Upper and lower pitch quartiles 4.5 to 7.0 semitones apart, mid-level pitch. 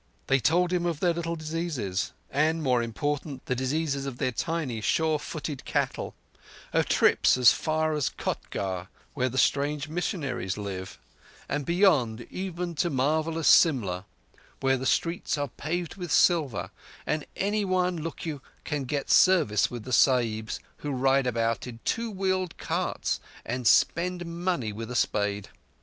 Yes: average, 5.2 semitones; medium, 145 Hz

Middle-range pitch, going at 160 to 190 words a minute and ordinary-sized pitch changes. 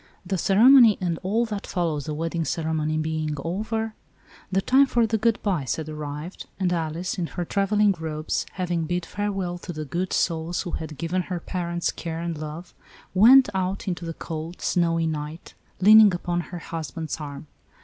Yes: medium, 175 Hz; average, 180 wpm; average, 3.3 semitones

